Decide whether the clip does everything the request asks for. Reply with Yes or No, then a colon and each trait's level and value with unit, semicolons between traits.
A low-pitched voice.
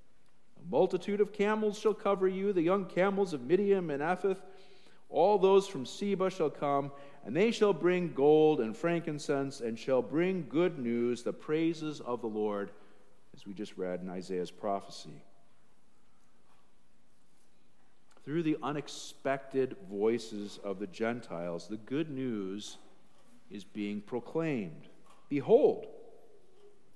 No: medium, 155 Hz